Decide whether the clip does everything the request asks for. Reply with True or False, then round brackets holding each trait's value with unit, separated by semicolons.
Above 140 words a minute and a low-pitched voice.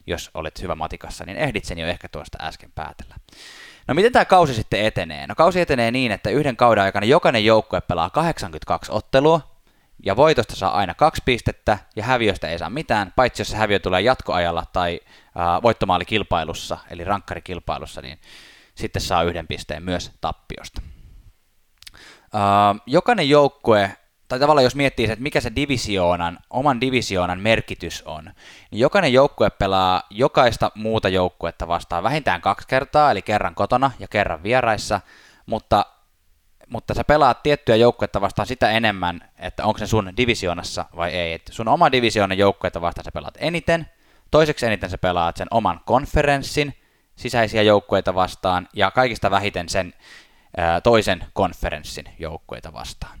True (150 wpm; 100 Hz)